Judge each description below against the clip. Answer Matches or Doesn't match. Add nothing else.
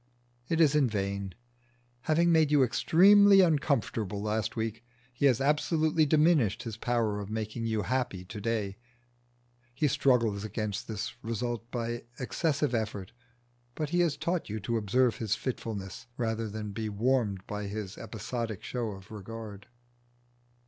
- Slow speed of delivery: Doesn't match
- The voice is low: Matches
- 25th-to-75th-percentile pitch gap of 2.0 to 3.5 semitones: Doesn't match